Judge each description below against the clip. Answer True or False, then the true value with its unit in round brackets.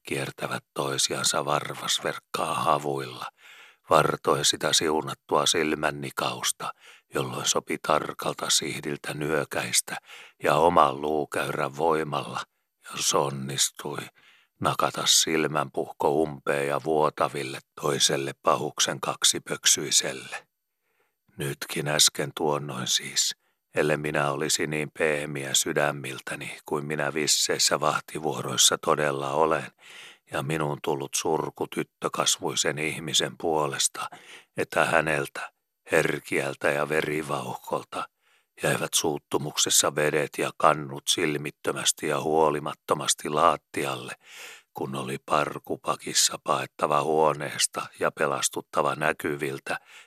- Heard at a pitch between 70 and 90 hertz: True (75 Hz)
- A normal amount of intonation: False (1.6 semitones)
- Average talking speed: False (90 wpm)